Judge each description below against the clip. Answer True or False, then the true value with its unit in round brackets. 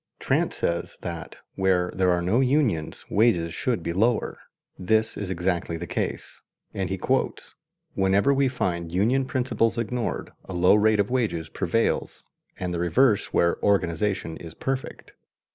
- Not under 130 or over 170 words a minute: True (150 wpm)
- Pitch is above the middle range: False (95 Hz)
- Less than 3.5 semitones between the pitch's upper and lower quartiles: False (5.0 semitones)